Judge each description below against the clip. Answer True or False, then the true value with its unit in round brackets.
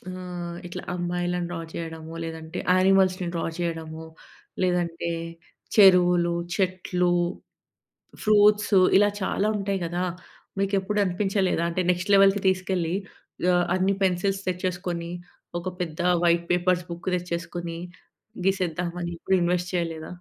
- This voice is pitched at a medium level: True (180 Hz)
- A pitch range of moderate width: False (1.7 semitones)